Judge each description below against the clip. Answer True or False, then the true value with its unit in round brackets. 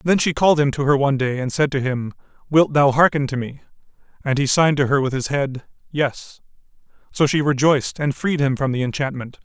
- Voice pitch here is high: False (140 Hz)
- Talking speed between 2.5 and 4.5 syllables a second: False (5.8 syllables/s)